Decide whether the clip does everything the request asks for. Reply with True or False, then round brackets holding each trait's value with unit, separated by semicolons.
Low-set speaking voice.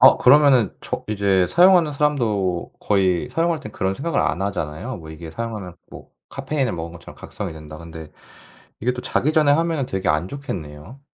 True (105 Hz)